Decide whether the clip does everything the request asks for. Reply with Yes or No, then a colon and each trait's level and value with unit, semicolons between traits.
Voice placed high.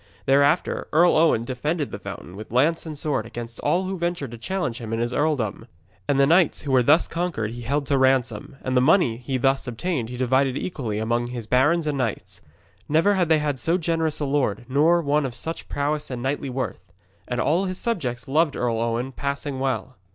No: low, 135 Hz